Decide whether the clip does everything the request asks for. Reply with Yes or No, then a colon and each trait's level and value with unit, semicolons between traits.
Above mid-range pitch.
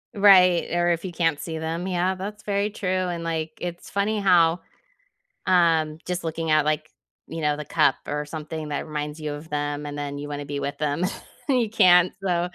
No: medium, 165 Hz